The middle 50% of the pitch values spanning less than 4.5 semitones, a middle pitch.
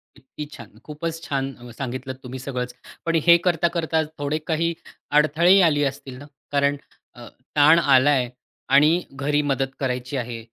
Yes: average, 3.3 semitones; medium, 145 Hz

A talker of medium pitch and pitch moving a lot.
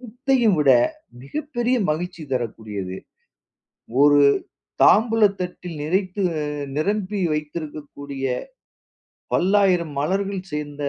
Yes: medium, 180 Hz; wide, 5.8 semitones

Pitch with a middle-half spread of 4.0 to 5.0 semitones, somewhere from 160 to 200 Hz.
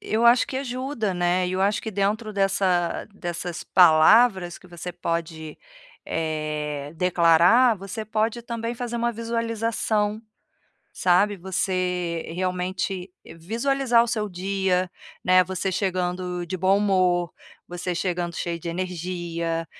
No: average, 3.6 semitones; medium, 185 Hz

